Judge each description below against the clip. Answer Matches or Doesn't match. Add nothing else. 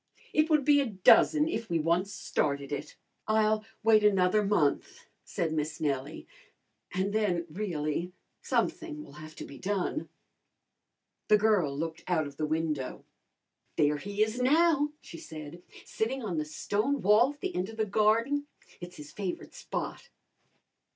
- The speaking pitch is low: Doesn't match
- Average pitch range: Doesn't match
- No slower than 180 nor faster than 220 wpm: Doesn't match